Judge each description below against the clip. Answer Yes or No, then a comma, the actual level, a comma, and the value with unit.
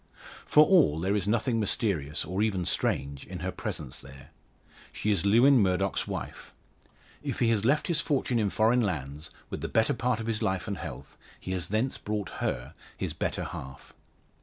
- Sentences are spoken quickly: No, average, 185 wpm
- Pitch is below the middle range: Yes, low, 105 Hz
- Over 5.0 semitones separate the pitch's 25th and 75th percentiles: Yes, wide, 5.6 semitones